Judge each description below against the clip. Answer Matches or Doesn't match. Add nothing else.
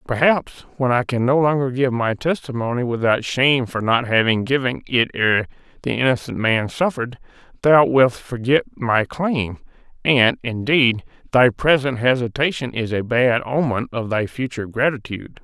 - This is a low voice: Matches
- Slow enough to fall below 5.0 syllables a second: Matches